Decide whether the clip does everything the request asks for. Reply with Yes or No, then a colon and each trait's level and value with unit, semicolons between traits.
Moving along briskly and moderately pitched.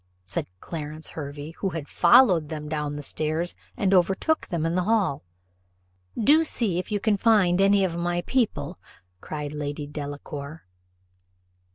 No: average, 145 wpm; medium, 170 Hz